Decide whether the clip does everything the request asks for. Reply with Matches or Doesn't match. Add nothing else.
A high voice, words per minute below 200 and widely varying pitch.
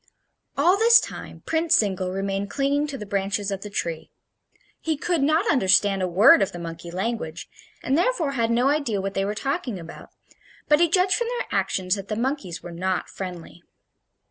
Matches